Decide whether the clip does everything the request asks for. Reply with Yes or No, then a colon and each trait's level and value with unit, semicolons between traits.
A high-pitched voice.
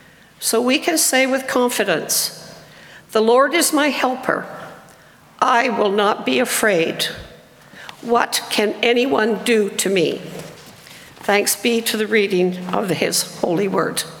Yes: high, 235 Hz